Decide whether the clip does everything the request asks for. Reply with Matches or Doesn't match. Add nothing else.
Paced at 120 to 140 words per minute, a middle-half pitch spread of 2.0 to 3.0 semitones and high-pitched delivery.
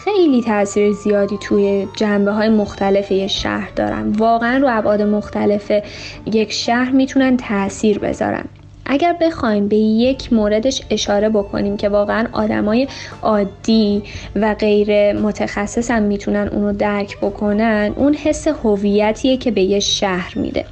Matches